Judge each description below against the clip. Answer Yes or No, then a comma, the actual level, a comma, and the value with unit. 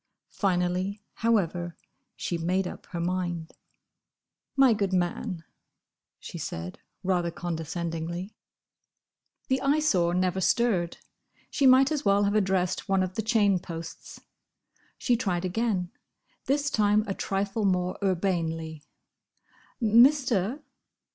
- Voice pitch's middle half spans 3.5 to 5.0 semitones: Yes, average, 3.8 semitones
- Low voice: No, high, 190 Hz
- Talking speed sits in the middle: No, slow, 110 wpm